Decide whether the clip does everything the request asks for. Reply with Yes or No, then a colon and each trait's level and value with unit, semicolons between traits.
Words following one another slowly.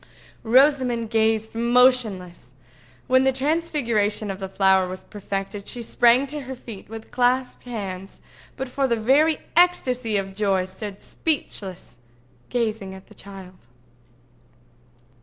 Yes: slow, 120 wpm